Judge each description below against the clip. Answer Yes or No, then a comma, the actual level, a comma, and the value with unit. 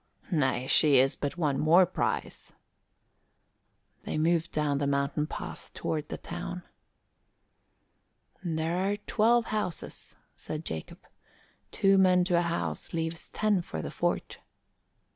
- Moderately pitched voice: Yes, medium, 165 Hz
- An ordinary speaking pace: No, slow, 125 wpm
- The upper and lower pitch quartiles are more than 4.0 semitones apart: No, average, 3.6 semitones